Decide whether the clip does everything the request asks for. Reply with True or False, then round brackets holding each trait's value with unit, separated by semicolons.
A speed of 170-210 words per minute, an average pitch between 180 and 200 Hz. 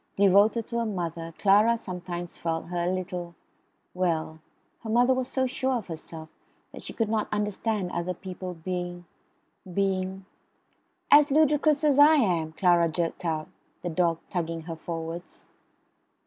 False (150 wpm; 185 Hz)